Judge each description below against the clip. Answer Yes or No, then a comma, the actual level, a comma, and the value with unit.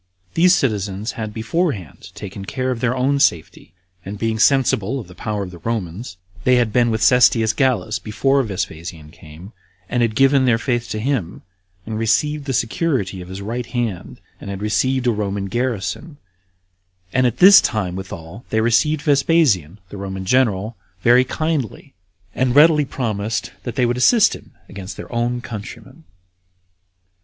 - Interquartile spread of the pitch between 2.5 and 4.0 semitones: No, average, 4.6 semitones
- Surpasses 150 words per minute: Yes, average, 165 wpm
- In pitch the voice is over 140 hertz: No, low, 115 Hz